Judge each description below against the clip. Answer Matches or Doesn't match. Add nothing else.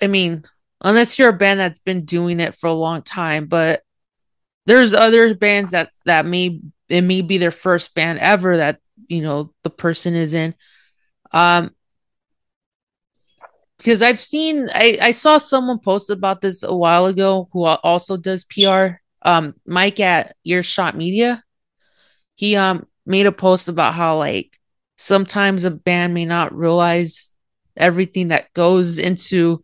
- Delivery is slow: Doesn't match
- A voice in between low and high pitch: Matches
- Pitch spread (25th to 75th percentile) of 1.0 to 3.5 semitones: Matches